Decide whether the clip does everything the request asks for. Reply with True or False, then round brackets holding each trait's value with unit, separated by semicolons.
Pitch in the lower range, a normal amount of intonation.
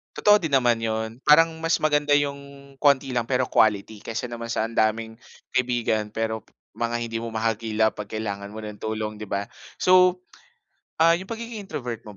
True (115 Hz; 4.9 semitones)